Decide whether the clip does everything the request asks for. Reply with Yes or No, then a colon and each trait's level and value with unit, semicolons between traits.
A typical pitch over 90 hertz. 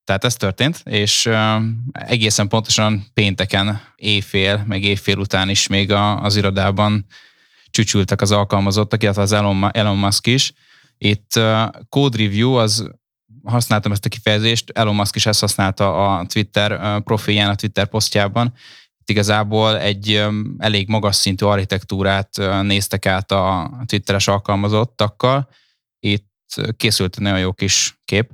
Yes: low, 105 Hz